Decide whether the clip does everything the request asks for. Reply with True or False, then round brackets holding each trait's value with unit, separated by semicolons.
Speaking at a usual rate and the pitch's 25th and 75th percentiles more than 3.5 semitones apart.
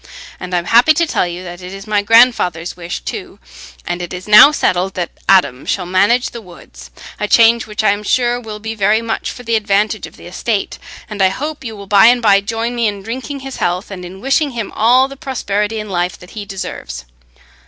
False (225 wpm; 4.2 semitones)